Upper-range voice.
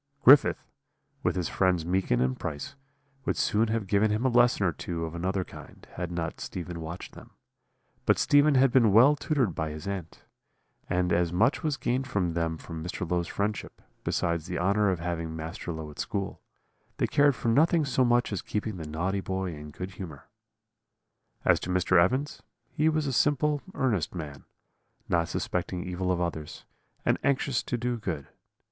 No: very low, 95 Hz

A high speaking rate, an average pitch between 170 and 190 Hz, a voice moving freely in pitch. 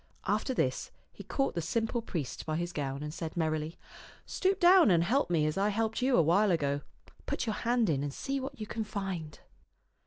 Yes: fast, 215 wpm; medium, 185 Hz; wide, 6.8 semitones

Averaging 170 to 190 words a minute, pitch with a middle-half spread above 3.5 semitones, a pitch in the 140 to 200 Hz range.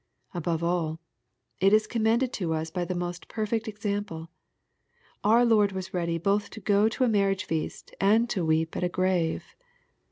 Yes: average, 180 wpm; average, 4.0 semitones; high, 190 Hz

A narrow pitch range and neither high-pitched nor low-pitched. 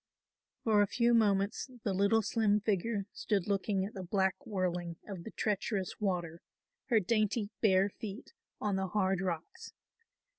No: narrow, 2.2 semitones; high, 200 Hz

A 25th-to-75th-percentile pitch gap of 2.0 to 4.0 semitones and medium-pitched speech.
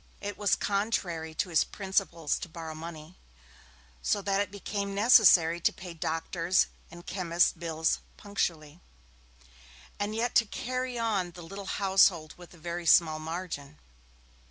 Yes: average, 3.5 semitones; medium, 175 Hz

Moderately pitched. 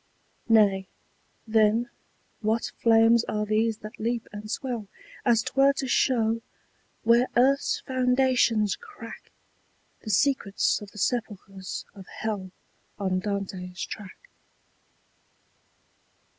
No: high, 220 Hz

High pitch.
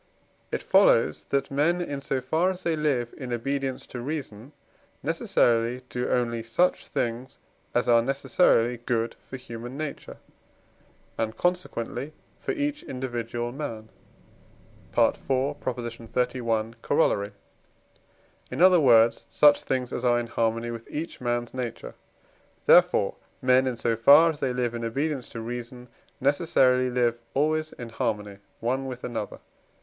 No: low, 125 Hz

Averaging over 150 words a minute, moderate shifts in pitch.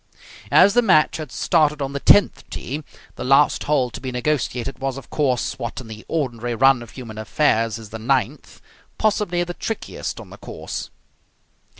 Yes: average, 180 wpm; average, 4.2 semitones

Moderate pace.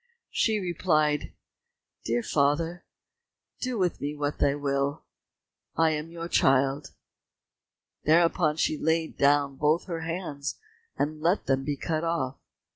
No: slow, 125 wpm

